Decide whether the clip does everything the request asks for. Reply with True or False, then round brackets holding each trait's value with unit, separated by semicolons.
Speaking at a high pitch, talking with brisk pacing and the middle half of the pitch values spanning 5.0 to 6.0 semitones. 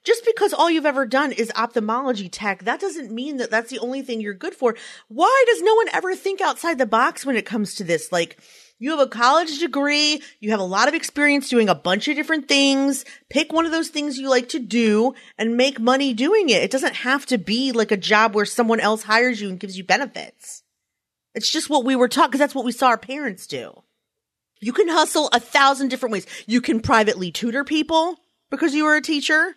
True (265 Hz; 230 wpm; 5.3 semitones)